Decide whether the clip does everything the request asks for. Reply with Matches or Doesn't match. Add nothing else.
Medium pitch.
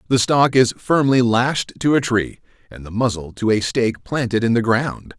Doesn't match